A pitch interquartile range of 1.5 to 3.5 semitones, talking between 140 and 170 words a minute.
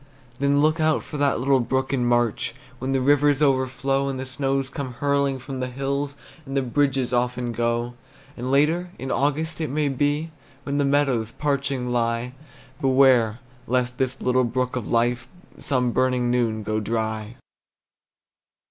Yes: narrow, 2.4 semitones; average, 160 wpm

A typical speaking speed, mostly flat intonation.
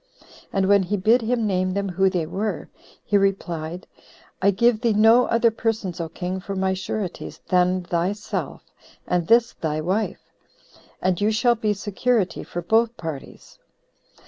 No: average, 155 wpm; average, 3.4 semitones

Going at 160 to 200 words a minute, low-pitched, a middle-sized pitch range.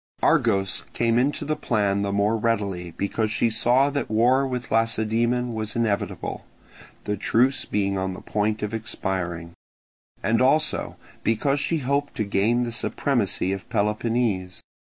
No: average, 145 wpm; low, 110 Hz; average, 3.4 semitones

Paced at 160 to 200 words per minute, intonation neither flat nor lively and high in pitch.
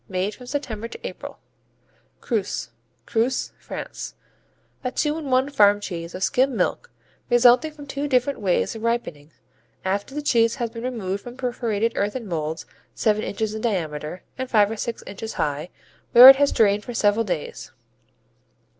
Yes: average, 165 wpm; average, 4.1 semitones; high, 225 Hz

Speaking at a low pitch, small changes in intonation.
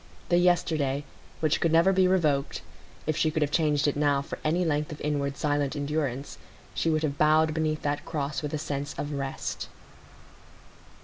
No: medium, 150 Hz; narrow, 1.7 semitones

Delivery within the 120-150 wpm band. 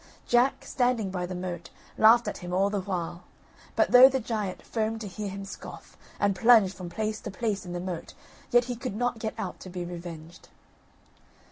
No: average, 200 wpm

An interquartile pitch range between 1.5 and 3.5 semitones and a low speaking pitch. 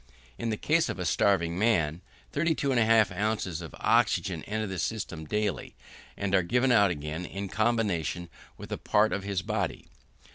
No: average, 4.2 semitones; low, 100 Hz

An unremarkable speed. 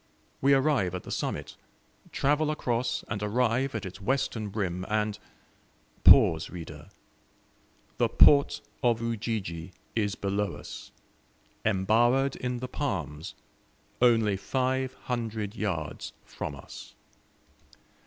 No: slow, 110 wpm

